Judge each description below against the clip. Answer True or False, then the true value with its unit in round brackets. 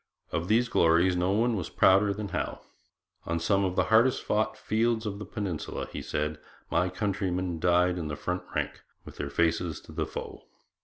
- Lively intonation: False (3.7 semitones)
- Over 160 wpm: True (190 wpm)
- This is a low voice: True (90 Hz)